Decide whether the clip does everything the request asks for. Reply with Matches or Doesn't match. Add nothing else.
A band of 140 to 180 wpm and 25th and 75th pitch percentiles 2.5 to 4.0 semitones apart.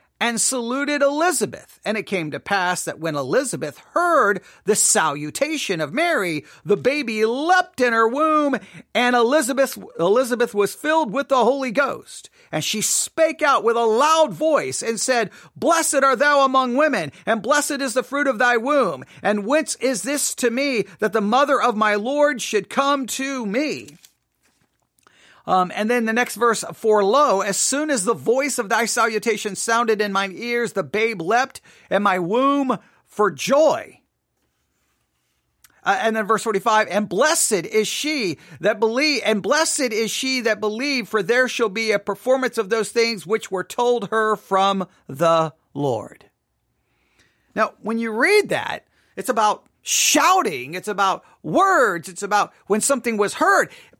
Doesn't match